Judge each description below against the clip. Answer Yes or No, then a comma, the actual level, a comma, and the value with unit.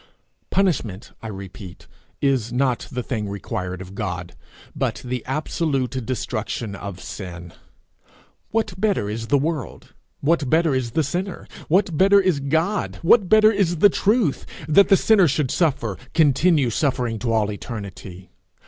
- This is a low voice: Yes, low, 130 Hz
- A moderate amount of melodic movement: No, wide, 8.1 semitones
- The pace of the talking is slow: No, average, 145 wpm